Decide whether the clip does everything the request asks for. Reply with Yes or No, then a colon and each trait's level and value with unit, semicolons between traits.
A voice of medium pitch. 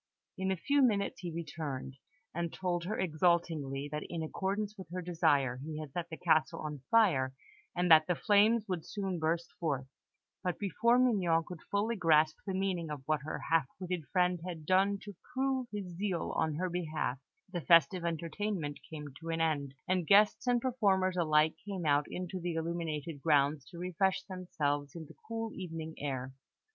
Yes: medium, 170 Hz